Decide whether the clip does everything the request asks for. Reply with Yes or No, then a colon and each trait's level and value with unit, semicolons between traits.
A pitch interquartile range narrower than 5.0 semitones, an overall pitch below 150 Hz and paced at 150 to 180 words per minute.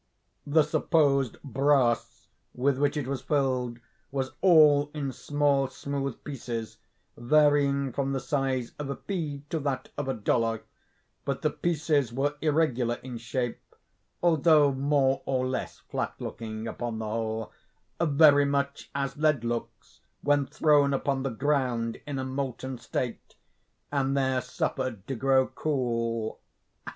No: average, 2.7 semitones; low, 135 Hz; average, 140 wpm